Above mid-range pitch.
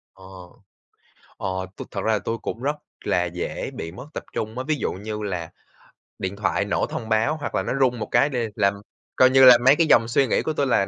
No: low, 115 Hz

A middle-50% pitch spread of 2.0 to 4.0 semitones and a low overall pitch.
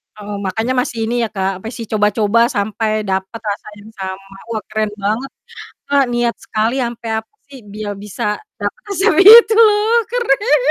No: average, 2.9 semitones; high, 220 Hz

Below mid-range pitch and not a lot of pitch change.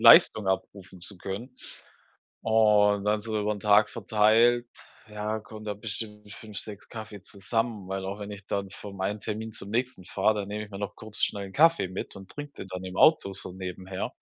Yes: low, 105 Hz; narrow, 1.8 semitones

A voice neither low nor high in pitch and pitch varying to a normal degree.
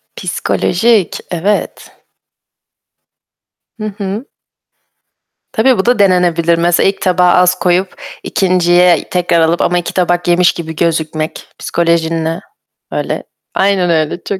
No: medium, 175 Hz; narrow, 2.1 semitones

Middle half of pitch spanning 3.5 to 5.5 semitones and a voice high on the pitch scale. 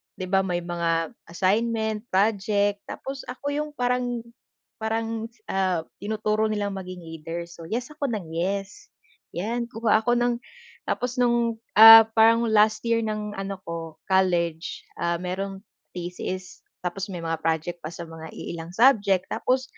Yes: average, 4.5 semitones; high, 200 Hz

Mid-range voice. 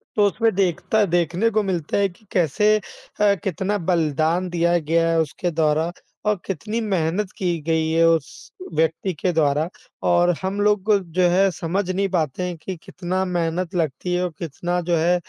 Yes: medium, 175 Hz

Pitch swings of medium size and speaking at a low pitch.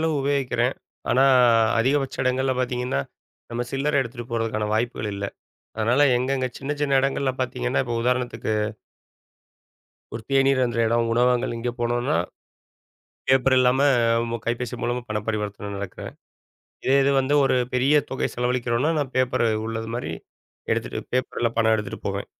No: narrow, 2.2 semitones; low, 125 Hz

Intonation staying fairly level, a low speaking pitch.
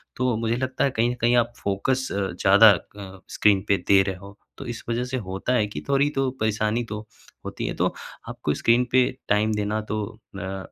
No: average, 3.6 semitones; low, 110 Hz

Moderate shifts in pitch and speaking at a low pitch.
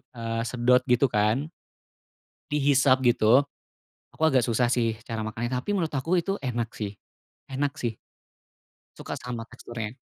Yes: average, 3.2 semitones; low, 125 Hz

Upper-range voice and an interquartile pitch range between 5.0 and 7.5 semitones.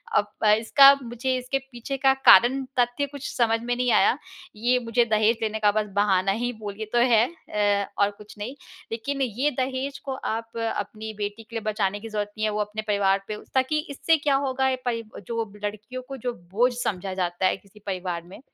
No: high, 225 Hz; average, 3.6 semitones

